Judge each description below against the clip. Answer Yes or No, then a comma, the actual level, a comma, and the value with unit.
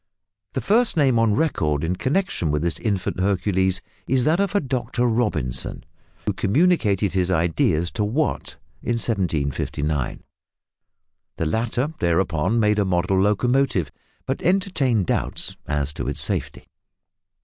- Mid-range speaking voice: No, low, 105 Hz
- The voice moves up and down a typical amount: No, wide, 7.1 semitones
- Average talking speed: No, slow, 130 wpm